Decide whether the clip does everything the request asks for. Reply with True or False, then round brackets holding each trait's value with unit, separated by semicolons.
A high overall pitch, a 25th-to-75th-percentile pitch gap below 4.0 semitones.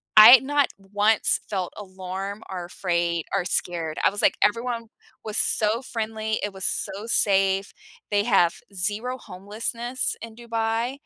True (210 Hz; 3.2 semitones)